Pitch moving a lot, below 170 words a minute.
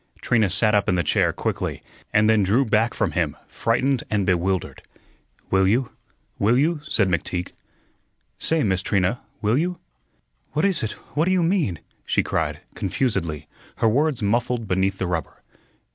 Yes: wide, 5.7 semitones; average, 160 wpm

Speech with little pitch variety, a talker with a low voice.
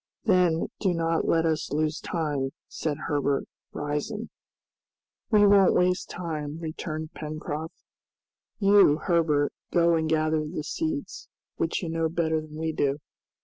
No: narrow, 2.1 semitones; medium, 160 Hz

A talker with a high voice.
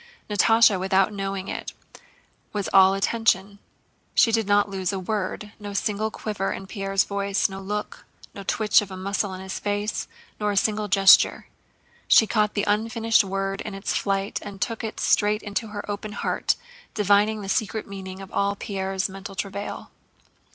Yes: high, 200 Hz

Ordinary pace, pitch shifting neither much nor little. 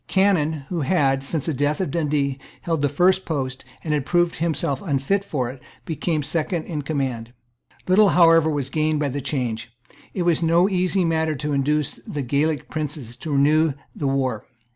Yes: average, 180 wpm; average, 3.3 semitones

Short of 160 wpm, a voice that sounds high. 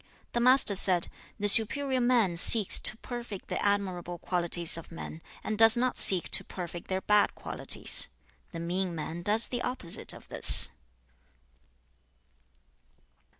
Yes: average, 145 wpm; high, 200 Hz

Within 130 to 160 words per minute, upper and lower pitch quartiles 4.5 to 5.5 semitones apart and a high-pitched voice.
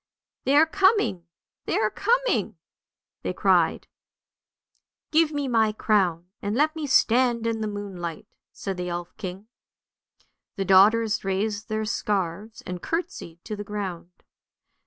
Yes: average, 145 wpm; average, 5.2 semitones; high, 210 Hz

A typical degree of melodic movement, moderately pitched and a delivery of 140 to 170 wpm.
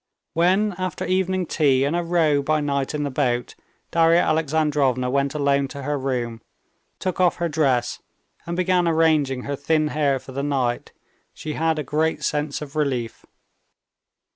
Yes: average, 3.0 semitones; medium, 150 Hz; average, 165 wpm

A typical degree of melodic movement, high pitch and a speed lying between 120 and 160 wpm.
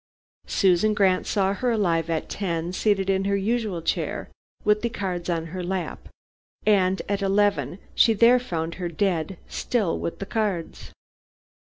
Yes: average, 3.1 semitones; high, 195 Hz; average, 155 wpm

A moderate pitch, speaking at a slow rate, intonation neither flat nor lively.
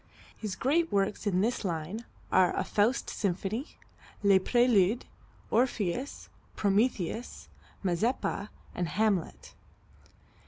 No: high, 205 Hz; slow, 95 wpm; average, 4.2 semitones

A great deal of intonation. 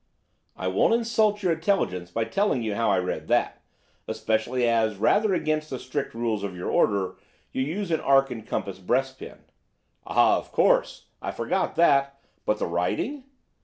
Yes: wide, 7.4 semitones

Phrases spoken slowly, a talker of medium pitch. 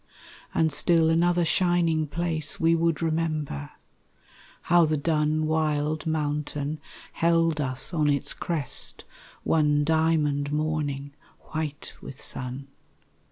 Yes: slow, 110 wpm; medium, 155 Hz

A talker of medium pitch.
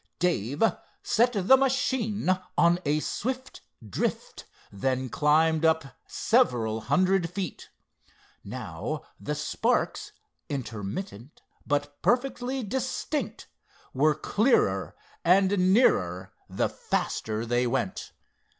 Yes: medium, 165 Hz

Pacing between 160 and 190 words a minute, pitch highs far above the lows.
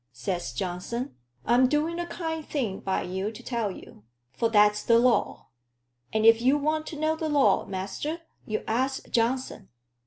Yes: average, 165 wpm; wide, 6.1 semitones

